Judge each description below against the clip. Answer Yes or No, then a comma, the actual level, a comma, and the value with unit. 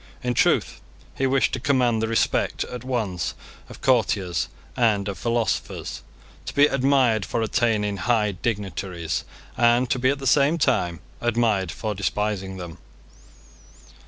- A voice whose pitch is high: No, low, 115 Hz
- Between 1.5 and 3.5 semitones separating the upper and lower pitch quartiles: No, average, 4.2 semitones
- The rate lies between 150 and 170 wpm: No, average, 140 wpm